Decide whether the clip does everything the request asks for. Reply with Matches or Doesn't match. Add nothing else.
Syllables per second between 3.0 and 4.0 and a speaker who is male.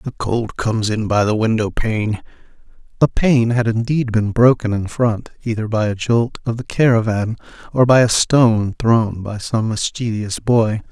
Doesn't match